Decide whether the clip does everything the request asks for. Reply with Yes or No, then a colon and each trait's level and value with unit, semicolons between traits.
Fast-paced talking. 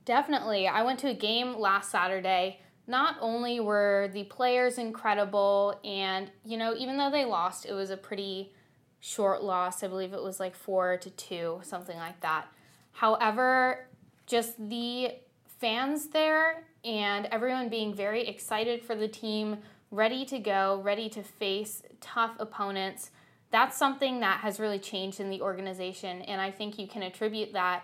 No: average, 160 wpm